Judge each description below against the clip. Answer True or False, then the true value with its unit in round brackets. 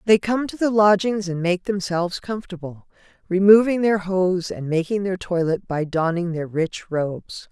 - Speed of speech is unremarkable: True (170 wpm)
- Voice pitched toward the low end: False (185 Hz)